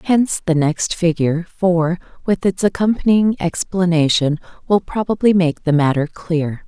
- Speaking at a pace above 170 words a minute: No, slow, 135 wpm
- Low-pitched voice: No, medium, 175 Hz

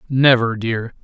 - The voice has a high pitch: No, low, 120 Hz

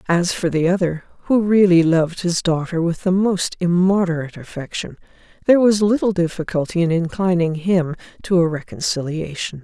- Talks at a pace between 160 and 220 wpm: No, average, 150 wpm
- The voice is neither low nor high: Yes, medium, 175 Hz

